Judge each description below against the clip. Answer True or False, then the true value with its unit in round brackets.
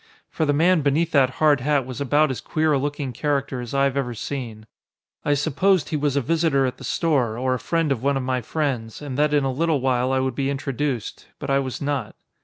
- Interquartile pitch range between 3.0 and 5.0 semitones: False (2.4 semitones)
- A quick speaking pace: True (240 wpm)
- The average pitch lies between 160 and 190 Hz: False (140 Hz)